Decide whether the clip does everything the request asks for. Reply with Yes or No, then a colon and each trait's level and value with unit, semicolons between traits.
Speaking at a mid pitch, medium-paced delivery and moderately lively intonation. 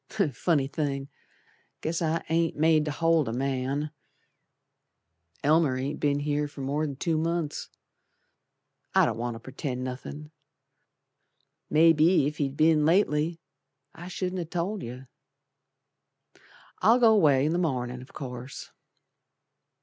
No: medium, 150 Hz; slow, 125 wpm; average, 3.4 semitones